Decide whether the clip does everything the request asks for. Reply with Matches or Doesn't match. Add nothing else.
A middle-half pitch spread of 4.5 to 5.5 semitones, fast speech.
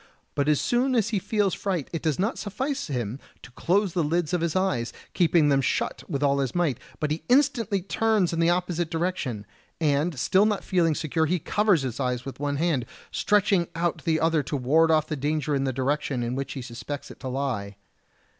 Matches